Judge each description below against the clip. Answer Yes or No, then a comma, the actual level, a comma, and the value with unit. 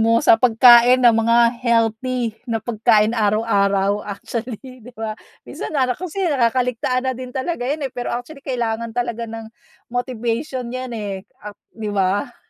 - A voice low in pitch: No, high, 235 Hz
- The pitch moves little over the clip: Yes, narrow, 2.3 semitones